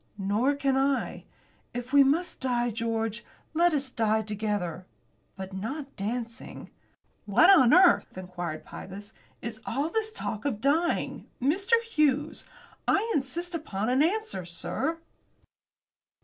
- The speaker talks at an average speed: No, slow, 125 wpm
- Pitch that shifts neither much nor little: No, wide, 6.5 semitones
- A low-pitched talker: No, very high, 255 Hz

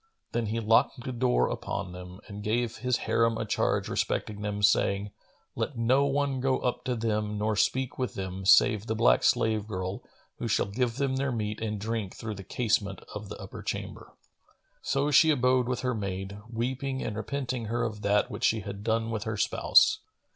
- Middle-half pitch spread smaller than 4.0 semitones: Yes, average, 3.5 semitones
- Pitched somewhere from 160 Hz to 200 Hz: No, low, 110 Hz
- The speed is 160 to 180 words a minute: No, average, 190 wpm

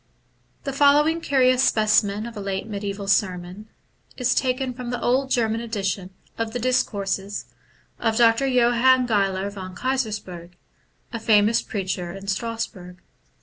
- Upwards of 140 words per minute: No, slow, 135 wpm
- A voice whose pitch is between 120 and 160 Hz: No, high, 220 Hz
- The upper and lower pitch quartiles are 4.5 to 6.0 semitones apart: No, average, 4.1 semitones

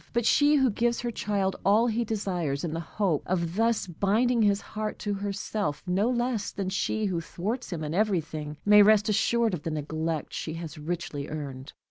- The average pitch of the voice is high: Yes, high, 195 Hz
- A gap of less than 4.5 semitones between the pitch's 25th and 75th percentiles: No, average, 5.0 semitones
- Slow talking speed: No, average, 190 wpm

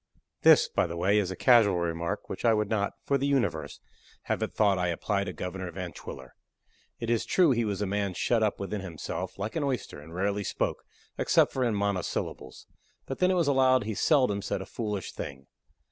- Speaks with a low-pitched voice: Yes, low, 105 Hz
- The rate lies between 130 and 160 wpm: No, fast, 205 wpm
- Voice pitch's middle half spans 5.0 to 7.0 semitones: No, average, 4.3 semitones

